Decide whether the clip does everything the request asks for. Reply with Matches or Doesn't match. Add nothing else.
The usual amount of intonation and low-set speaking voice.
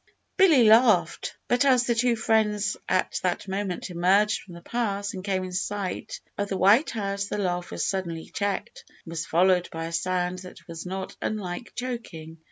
Doesn't match